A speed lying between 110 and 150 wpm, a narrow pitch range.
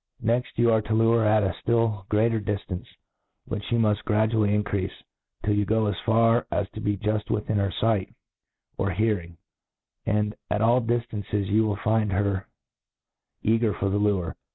No: average, 185 wpm; narrow, 1.7 semitones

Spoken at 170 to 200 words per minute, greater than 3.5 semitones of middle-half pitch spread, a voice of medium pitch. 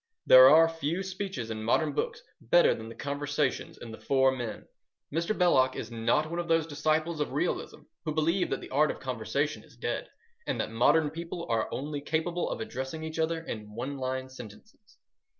Yes: average, 190 wpm; average, 4.2 semitones; medium, 145 Hz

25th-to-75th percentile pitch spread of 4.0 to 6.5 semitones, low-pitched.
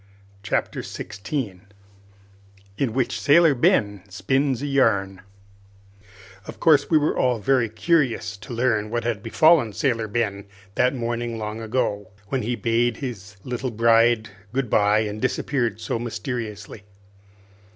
No: average, 3.3 semitones; low, 115 Hz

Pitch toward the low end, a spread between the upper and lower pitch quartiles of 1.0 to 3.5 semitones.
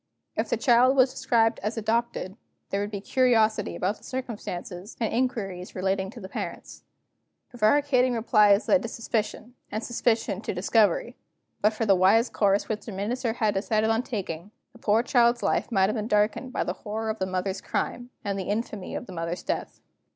No: high, 220 Hz; average, 3.2 semitones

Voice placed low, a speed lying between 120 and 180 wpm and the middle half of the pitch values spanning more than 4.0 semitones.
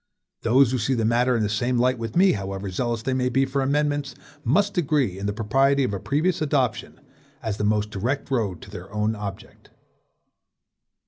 No: low, 120 Hz; average, 195 wpm; average, 4.5 semitones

